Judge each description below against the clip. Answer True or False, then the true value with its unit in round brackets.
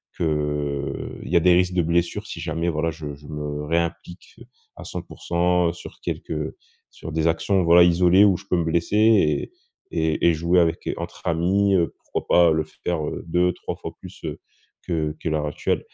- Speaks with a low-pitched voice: True (85 Hz)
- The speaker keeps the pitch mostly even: True (2.2 semitones)